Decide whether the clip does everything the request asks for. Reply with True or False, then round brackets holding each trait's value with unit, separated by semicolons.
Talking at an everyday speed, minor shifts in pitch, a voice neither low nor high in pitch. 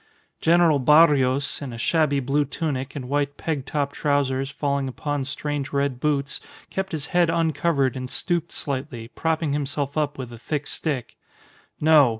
True (155 wpm; 2.3 semitones; 145 Hz)